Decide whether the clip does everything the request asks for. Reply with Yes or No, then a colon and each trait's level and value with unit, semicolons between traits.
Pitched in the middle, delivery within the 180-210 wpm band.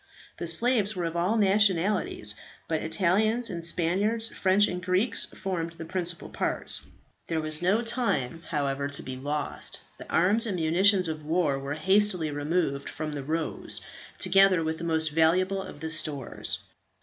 No: medium, 170 Hz; average, 160 wpm